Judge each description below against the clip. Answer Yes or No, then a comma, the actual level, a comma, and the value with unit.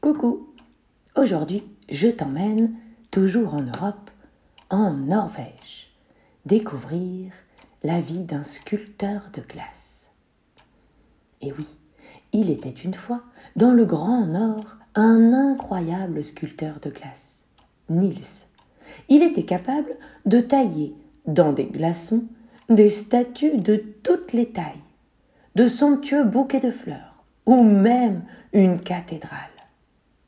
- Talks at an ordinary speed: No, slow, 110 wpm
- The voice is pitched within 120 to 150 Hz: No, high, 210 Hz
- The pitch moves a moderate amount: No, wide, 6.0 semitones